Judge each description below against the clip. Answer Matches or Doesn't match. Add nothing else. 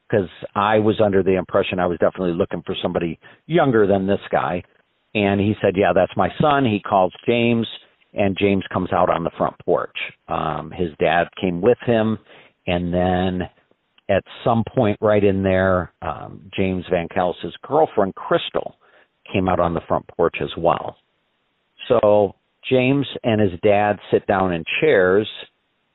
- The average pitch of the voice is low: Matches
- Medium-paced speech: Matches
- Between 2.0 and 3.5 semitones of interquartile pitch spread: Matches